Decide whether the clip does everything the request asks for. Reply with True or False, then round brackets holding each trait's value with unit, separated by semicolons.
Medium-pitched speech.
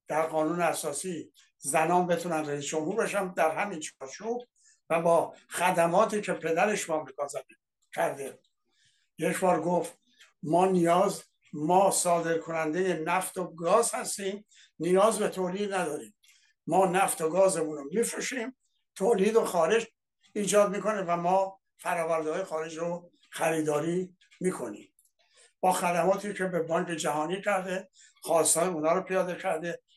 True (180 Hz)